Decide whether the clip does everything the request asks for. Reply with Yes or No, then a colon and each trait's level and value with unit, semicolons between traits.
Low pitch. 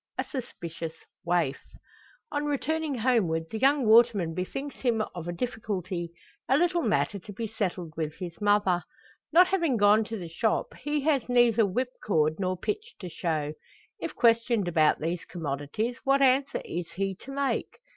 No: high, 215 Hz